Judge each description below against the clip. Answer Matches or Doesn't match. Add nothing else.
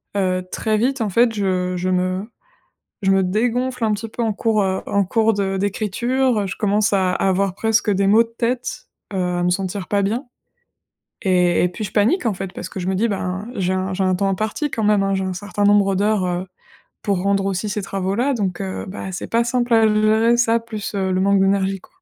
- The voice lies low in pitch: Doesn't match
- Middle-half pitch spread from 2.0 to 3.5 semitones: Matches